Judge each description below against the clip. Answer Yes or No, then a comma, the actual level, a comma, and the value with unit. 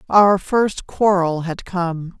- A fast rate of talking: No, slow, 135 wpm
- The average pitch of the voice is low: No, medium, 185 Hz